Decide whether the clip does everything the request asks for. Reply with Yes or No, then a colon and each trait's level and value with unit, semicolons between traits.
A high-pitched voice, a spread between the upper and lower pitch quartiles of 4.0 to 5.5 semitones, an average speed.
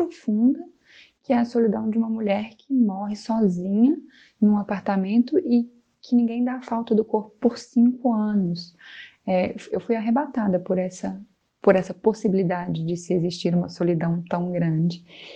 Yes: high, 215 Hz; average, 4.6 semitones; average, 155 wpm